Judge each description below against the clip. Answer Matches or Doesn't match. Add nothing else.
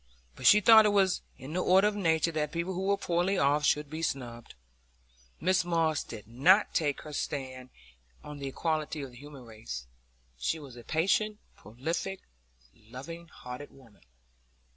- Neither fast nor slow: Matches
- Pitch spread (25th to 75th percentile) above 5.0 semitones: Matches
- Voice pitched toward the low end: Doesn't match